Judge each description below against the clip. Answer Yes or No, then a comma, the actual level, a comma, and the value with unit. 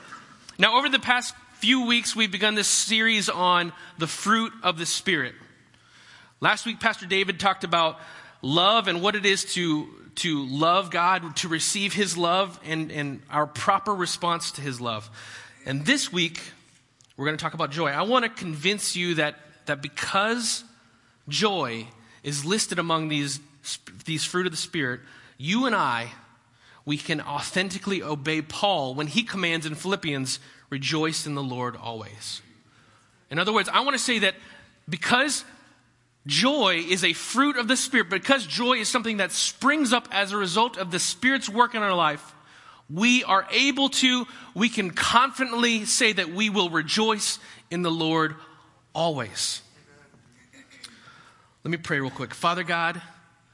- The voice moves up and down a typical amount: No, wide, 6.4 semitones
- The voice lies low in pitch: No, medium, 175 Hz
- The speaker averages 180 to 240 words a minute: No, average, 160 wpm